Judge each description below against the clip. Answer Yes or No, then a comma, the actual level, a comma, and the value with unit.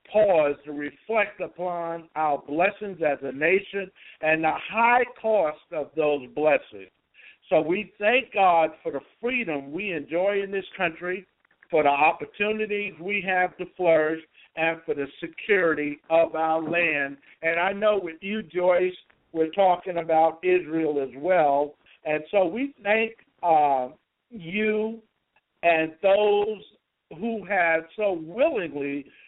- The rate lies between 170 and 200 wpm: No, slow, 135 wpm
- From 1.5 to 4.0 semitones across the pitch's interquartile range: No, average, 4.5 semitones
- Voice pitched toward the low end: No, medium, 175 Hz